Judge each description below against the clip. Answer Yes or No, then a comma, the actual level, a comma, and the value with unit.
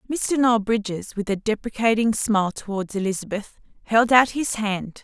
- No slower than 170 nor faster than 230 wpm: No, average, 155 wpm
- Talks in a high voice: Yes, high, 220 Hz